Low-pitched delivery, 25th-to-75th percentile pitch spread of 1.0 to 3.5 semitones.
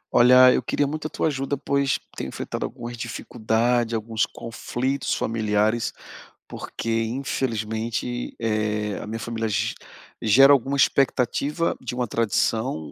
Yes: low, 120 Hz; average, 3.1 semitones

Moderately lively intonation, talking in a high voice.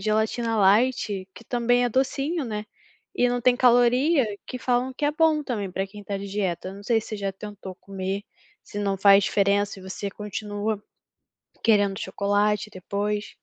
Yes: average, 3.6 semitones; high, 210 Hz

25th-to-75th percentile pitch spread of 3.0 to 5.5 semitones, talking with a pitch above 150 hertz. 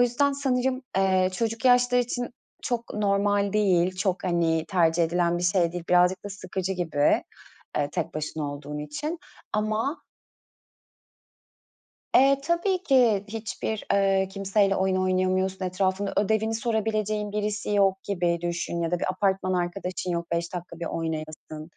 Yes: average, 3.7 semitones; high, 190 Hz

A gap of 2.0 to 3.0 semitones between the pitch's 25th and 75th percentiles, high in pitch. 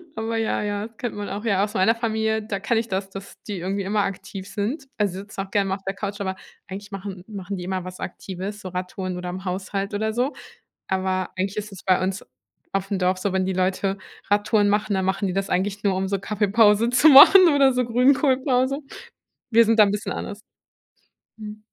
Yes: narrow, 2.4 semitones; high, 200 Hz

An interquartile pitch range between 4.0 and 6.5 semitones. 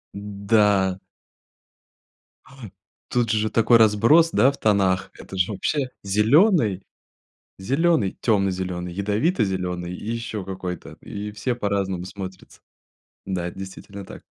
No: average, 3.3 semitones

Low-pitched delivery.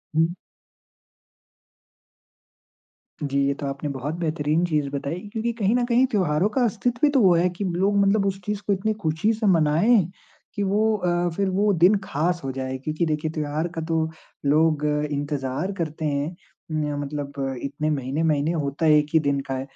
No: medium, 160 Hz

